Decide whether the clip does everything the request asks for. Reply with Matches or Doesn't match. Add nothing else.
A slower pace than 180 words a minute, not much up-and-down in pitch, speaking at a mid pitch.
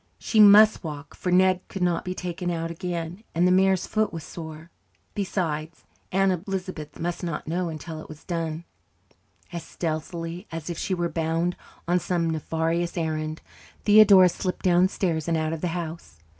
Matches